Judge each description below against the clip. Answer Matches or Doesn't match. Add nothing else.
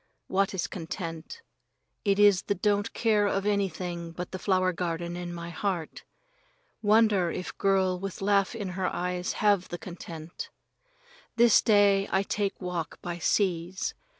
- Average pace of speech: Matches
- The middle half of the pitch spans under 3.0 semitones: Matches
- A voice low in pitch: Doesn't match